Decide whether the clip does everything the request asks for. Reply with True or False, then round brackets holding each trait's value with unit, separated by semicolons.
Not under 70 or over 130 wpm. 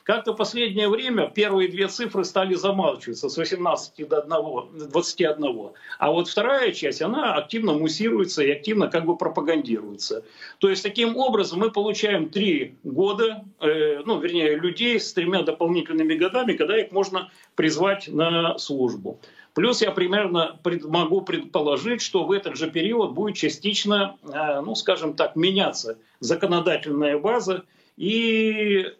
False (145 wpm)